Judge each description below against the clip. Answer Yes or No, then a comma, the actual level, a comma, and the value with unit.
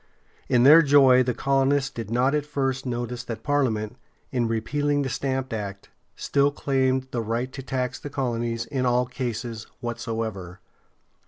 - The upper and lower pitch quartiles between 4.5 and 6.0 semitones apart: No, average, 2.8 semitones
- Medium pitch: No, low, 125 Hz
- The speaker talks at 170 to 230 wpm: No, average, 155 wpm